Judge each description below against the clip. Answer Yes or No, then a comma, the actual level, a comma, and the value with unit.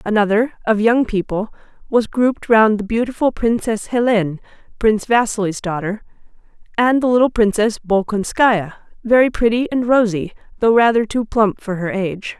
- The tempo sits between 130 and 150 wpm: Yes, average, 145 wpm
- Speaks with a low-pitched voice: No, high, 220 Hz